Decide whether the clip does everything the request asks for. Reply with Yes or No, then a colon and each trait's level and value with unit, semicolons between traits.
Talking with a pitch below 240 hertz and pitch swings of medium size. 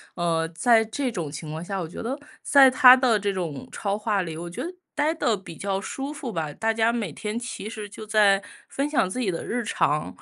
No: high, 210 Hz; wide, 5.7 semitones